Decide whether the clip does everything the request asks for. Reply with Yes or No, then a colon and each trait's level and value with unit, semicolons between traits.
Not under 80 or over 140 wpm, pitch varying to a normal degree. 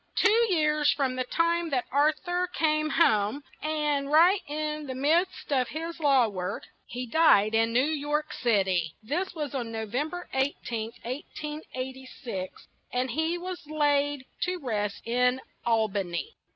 No: average, 160 wpm; average, 4.6 semitones